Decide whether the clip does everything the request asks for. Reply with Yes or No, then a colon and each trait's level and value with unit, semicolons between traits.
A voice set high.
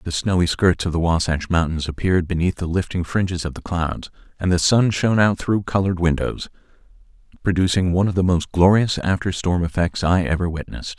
No: very low, 90 Hz